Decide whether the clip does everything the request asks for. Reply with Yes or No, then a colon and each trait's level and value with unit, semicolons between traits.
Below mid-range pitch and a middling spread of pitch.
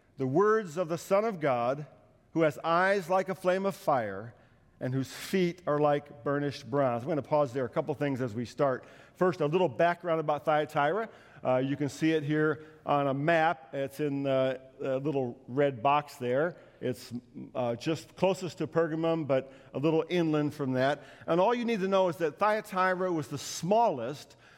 No: medium, 150 Hz; average, 4.2 semitones